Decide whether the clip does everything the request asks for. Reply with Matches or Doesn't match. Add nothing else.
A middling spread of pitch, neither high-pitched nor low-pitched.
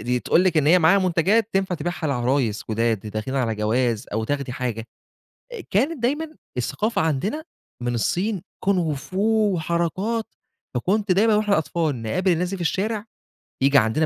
Doesn't match